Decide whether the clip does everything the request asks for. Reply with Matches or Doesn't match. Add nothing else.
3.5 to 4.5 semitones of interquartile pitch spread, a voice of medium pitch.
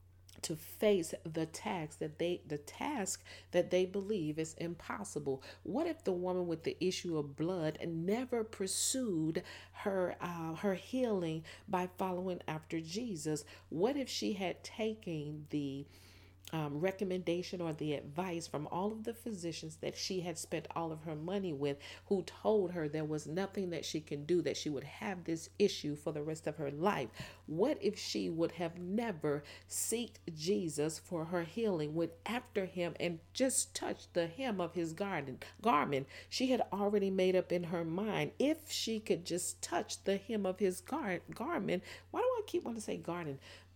Matches